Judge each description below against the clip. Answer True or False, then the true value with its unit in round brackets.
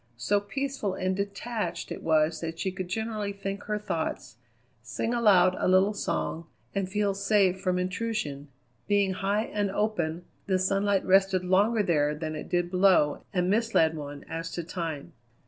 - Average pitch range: True (3.5 semitones)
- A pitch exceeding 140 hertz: True (190 Hz)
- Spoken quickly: False (165 wpm)